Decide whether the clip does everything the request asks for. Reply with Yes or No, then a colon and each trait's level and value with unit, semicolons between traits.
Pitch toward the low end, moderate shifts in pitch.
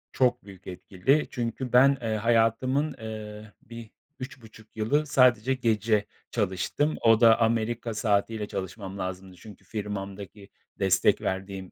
Yes: low, 110 Hz; average, 3.1 semitones